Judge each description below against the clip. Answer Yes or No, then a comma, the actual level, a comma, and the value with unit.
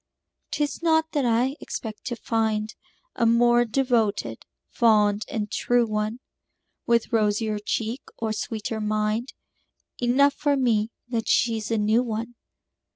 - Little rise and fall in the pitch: Yes, narrow, 2.2 semitones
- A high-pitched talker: Yes, high, 230 Hz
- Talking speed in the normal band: No, slow, 130 wpm